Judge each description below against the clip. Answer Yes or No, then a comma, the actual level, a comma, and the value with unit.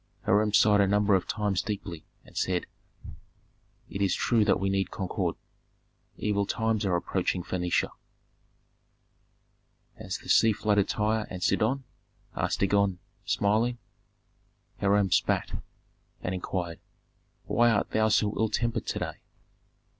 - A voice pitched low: Yes, low, 100 Hz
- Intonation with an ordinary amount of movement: No, narrow, 2.3 semitones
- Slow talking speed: Yes, slow, 130 wpm